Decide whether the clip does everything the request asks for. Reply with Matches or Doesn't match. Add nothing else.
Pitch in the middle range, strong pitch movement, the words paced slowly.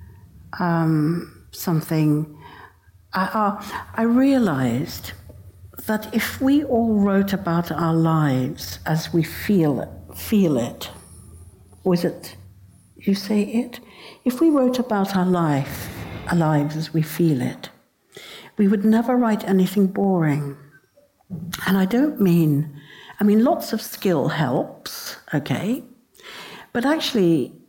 Matches